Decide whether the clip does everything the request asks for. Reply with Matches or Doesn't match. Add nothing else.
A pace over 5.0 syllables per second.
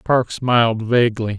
Doesn't match